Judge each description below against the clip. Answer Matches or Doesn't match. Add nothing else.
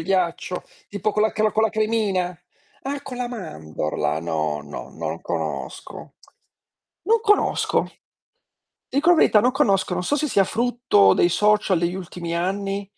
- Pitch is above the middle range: Matches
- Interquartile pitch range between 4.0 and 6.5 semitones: Matches